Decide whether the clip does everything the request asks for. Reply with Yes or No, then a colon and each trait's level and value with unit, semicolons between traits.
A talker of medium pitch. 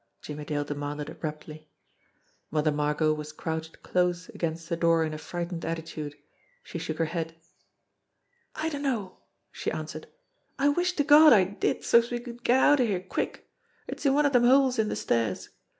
Yes: medium, 170 Hz